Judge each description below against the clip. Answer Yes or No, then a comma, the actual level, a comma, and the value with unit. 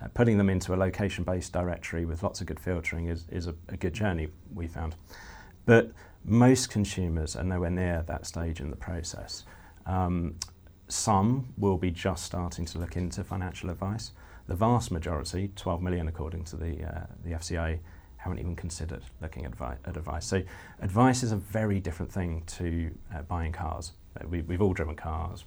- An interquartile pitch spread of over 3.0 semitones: No, narrow, 2.5 semitones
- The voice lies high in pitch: No, very low, 90 Hz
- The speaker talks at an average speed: Yes, average, 175 wpm